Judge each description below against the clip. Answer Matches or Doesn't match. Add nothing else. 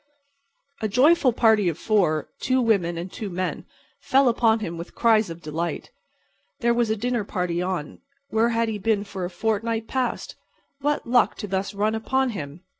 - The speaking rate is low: Doesn't match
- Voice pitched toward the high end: Matches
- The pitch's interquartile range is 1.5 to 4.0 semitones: Doesn't match